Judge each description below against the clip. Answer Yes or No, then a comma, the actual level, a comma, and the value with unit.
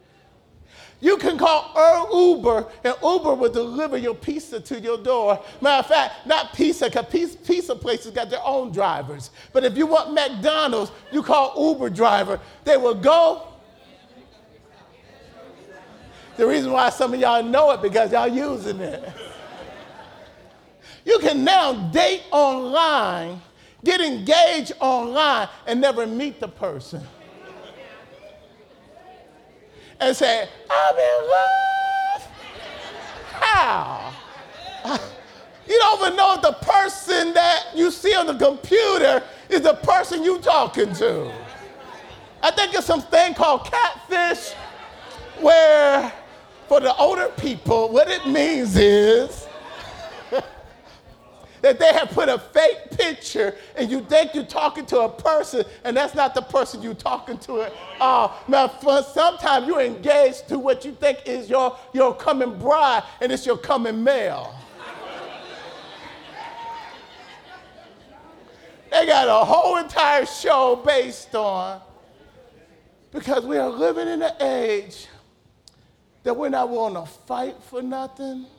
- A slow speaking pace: Yes, slow, 130 wpm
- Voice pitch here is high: Yes, very high, 280 Hz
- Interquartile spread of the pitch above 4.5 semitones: Yes, average, 5.2 semitones